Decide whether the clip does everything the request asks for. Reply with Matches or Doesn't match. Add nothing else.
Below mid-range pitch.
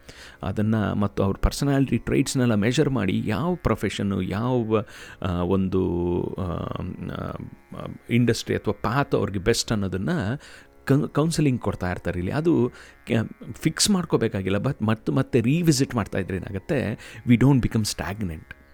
Matches